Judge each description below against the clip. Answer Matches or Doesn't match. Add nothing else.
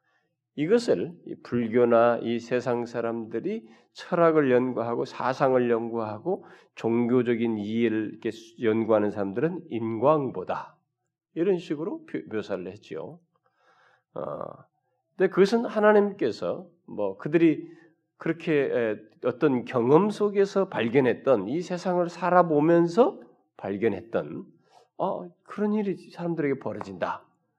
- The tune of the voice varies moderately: Doesn't match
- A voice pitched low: Doesn't match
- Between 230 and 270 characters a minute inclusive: Matches